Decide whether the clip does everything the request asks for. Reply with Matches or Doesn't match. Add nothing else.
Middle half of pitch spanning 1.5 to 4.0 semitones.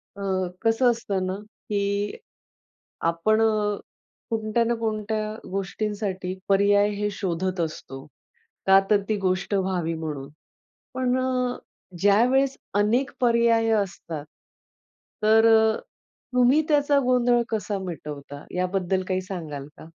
Matches